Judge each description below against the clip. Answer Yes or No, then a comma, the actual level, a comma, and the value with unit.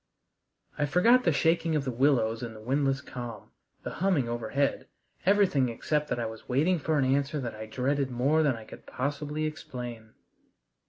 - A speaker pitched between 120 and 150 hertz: Yes, low, 135 Hz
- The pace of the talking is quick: No, average, 175 wpm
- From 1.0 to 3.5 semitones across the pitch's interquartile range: No, average, 4.2 semitones